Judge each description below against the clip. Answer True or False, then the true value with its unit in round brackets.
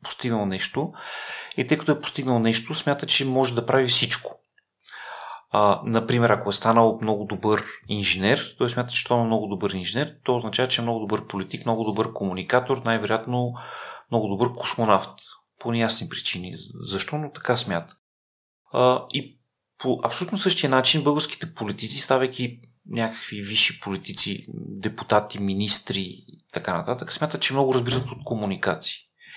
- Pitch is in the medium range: False (120 Hz)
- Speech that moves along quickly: False (150 wpm)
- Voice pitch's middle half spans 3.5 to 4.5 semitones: True (3.8 semitones)